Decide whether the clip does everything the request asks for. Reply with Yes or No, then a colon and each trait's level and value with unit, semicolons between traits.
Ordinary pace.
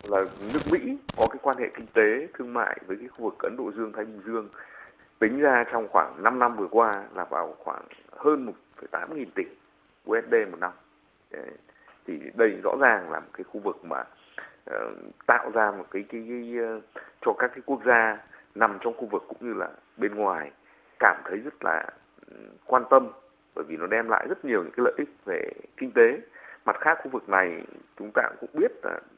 Yes: average, 205 wpm